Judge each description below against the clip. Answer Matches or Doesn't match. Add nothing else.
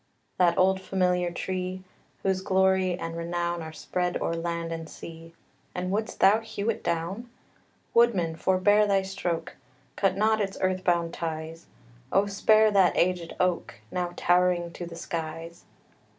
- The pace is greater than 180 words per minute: Doesn't match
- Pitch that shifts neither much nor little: Doesn't match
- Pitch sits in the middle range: Matches